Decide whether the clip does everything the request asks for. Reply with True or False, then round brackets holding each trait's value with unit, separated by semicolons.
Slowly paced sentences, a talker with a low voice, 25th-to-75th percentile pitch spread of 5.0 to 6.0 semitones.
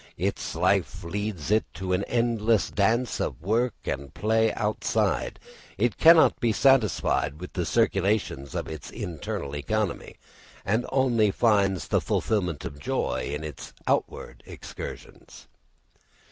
True (130 wpm; 105 Hz; 5.3 semitones)